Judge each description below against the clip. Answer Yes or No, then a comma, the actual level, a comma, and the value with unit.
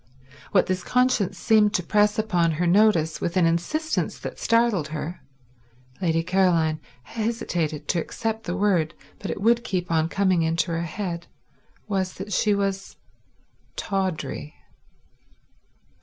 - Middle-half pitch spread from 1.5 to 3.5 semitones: No, average, 4.1 semitones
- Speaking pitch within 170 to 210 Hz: Yes, medium, 185 Hz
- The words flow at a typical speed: No, slow, 125 wpm